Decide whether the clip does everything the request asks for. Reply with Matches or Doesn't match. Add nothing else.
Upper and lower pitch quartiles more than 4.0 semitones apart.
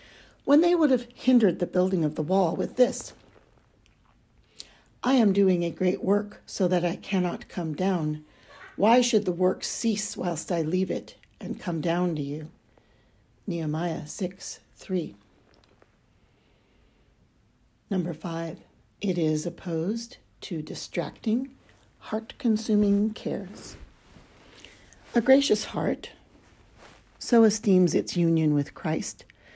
Matches